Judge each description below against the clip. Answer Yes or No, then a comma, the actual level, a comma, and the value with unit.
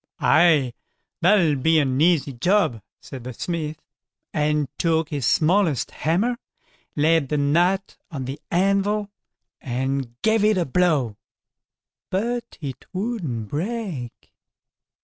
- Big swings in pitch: Yes, wide, 5.8 semitones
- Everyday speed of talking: No, slow, 115 wpm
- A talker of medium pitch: Yes, medium, 160 Hz